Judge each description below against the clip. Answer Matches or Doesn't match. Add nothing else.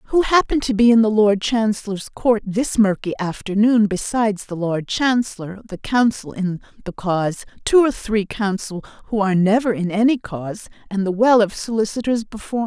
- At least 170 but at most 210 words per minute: Matches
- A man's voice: Doesn't match